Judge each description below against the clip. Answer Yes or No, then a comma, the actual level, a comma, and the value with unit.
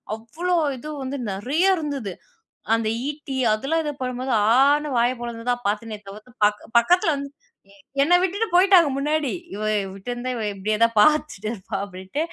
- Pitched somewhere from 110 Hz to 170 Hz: No, very high, 255 Hz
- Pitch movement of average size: No, wide, 5.8 semitones